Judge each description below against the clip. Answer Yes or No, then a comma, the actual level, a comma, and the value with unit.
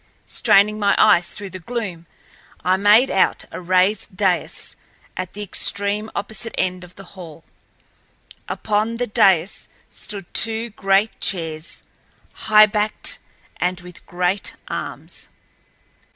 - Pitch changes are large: No, average, 2.7 semitones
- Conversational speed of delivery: No, slow, 120 wpm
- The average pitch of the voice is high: Yes, high, 195 Hz